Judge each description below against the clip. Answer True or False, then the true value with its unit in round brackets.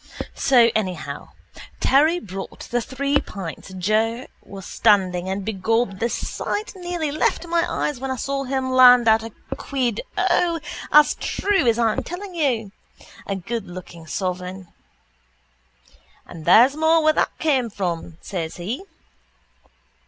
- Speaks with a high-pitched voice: True (235 Hz)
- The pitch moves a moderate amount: False (6.8 semitones)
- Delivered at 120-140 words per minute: True (135 wpm)